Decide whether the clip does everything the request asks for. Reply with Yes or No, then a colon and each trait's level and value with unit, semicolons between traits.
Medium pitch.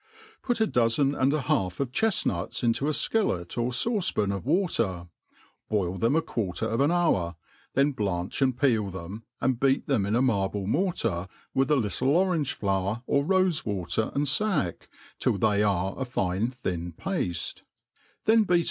No: low, 120 Hz